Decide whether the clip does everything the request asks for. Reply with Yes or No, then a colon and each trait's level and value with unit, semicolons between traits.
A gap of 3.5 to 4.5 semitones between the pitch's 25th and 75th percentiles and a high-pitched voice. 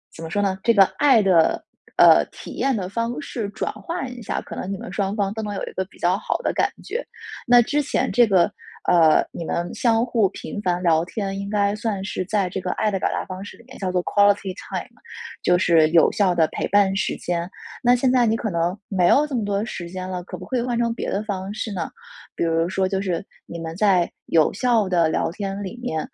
Yes: average, 3.8 semitones; high, 195 Hz